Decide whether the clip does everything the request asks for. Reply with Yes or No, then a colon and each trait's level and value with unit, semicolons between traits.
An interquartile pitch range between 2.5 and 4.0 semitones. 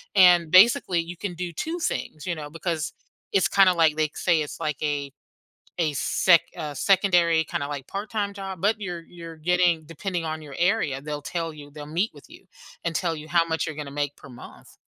Yes: average, 3.2 semitones